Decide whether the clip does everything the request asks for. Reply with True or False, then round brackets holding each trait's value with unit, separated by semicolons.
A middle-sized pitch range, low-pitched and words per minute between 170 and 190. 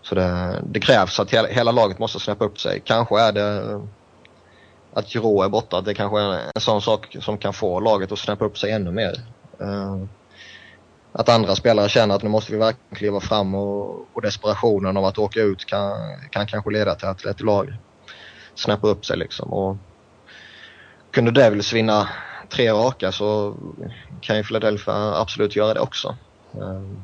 False (1.6 semitones; 105 Hz; 175 wpm)